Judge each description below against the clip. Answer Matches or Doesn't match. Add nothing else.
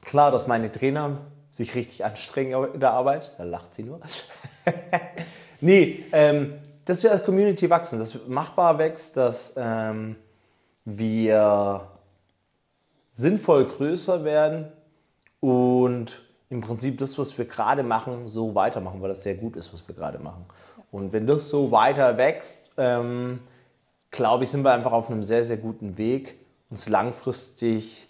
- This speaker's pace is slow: Doesn't match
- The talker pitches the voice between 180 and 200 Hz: Doesn't match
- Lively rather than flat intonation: Doesn't match